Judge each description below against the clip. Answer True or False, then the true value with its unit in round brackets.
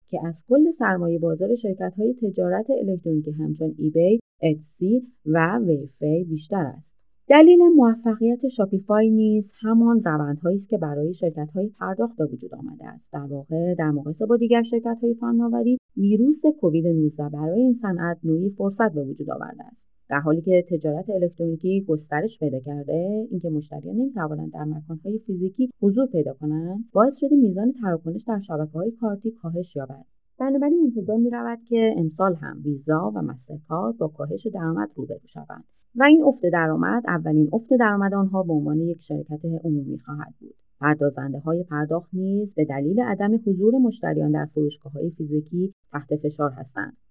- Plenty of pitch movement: True (6.7 semitones)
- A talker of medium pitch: True (175 Hz)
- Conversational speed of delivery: False (160 wpm)